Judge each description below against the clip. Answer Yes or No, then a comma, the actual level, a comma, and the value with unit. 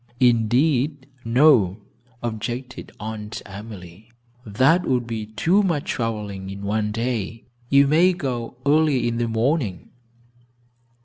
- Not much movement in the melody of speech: No, average, 4.4 semitones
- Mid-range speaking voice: No, low, 115 Hz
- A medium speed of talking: No, slow, 115 wpm